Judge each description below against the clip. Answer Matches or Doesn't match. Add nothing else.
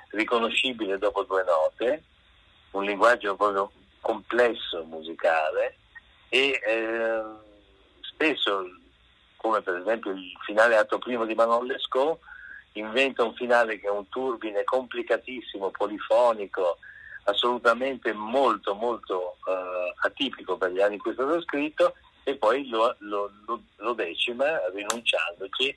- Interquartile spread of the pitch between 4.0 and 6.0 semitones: Matches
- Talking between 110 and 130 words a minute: Matches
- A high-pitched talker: Doesn't match